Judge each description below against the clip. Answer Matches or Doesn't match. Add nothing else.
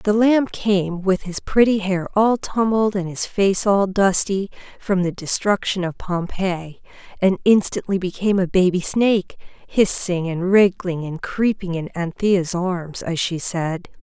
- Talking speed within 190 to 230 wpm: Doesn't match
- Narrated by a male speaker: Doesn't match